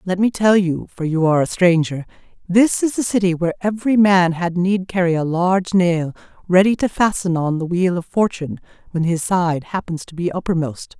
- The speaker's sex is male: No, female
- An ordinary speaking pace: Yes, average, 190 wpm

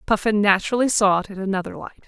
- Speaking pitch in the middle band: No, high, 205 Hz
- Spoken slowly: No, fast, 205 wpm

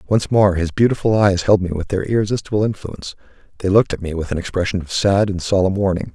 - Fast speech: Yes, fast, 225 wpm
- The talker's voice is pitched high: No, very low, 95 Hz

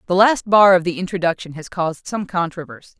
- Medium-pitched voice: Yes, medium, 180 Hz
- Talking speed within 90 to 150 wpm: No, average, 200 wpm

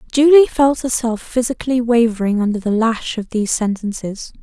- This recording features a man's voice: No, female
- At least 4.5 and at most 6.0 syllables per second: Yes, 5.4 syllables/s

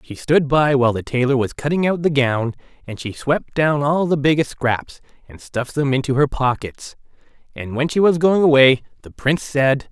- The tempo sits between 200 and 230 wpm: Yes, fast, 205 wpm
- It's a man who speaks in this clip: Yes, male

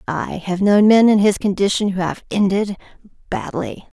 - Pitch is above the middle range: Yes, high, 195 Hz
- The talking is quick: No, average, 165 wpm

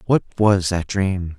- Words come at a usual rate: Yes, average, 175 wpm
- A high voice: No, very low, 95 Hz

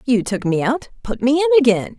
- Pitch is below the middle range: No, very high, 260 Hz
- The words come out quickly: Yes, fast, 210 wpm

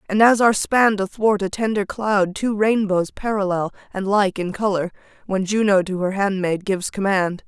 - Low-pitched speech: No, high, 200 Hz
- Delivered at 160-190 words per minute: Yes, average, 175 wpm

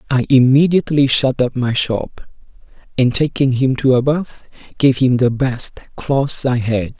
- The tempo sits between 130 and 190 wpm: Yes, average, 165 wpm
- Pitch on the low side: Yes, low, 130 Hz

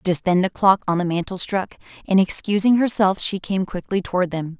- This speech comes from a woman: Yes, female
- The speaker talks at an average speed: No, fast, 210 wpm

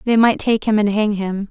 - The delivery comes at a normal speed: No, fast, 280 wpm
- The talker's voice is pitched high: Yes, high, 215 Hz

